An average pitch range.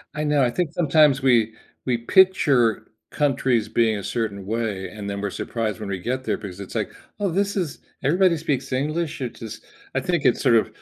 No: wide, 5.7 semitones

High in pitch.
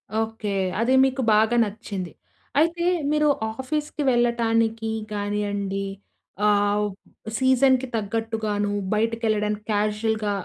Yes: high, 220 Hz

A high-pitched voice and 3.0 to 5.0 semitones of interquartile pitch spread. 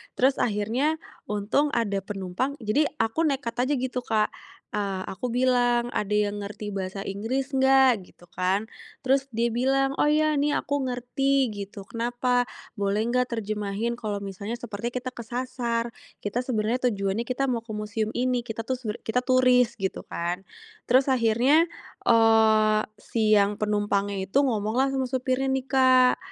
Yes: high, 235 Hz; average, 3.6 semitones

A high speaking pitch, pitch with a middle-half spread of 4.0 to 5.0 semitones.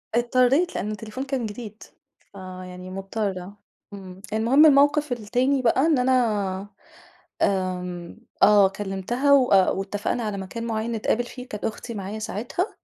Yes: high, 215 Hz; average, 4.4 semitones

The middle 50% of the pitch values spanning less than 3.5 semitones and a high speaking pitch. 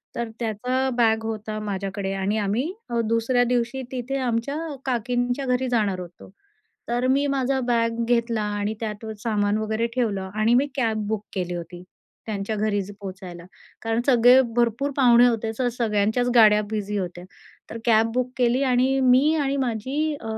Yes: average, 3.0 semitones; high, 230 Hz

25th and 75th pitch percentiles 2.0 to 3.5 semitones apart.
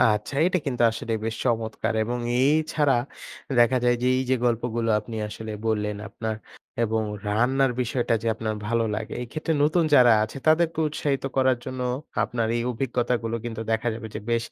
Yes: average, 2.7 semitones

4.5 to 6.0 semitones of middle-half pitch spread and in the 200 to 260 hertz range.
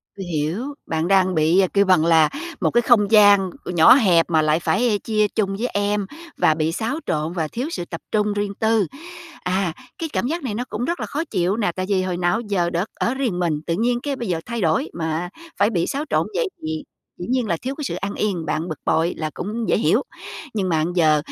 No: average, 5.1 semitones; high, 190 Hz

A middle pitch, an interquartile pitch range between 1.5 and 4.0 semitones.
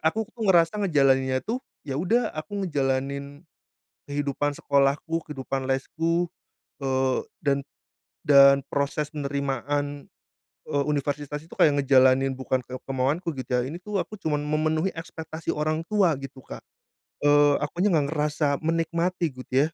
Yes: medium, 145 Hz; average, 3.0 semitones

